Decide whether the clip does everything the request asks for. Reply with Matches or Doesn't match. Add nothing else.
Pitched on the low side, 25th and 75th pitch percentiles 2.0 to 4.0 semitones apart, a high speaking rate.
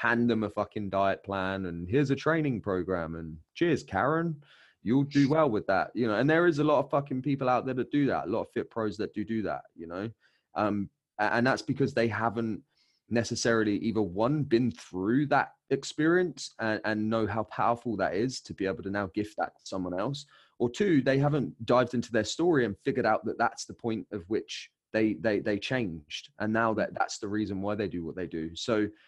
Doesn't match